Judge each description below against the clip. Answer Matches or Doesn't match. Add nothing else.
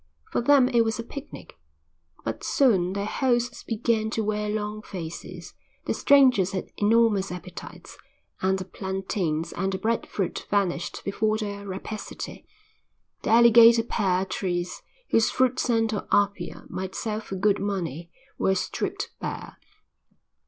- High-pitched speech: Matches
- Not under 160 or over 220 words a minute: Doesn't match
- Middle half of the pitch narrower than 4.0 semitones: Matches